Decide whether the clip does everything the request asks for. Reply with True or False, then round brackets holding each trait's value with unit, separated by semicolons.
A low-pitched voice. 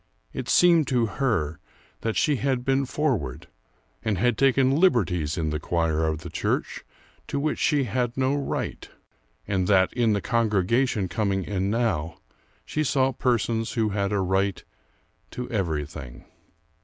True (110 Hz)